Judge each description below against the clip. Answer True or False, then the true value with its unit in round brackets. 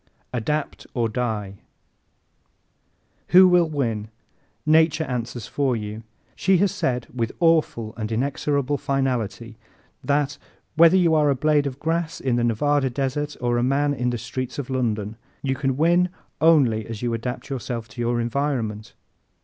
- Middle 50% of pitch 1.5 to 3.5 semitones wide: False (4.2 semitones)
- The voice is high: False (130 Hz)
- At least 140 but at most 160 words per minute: True (155 wpm)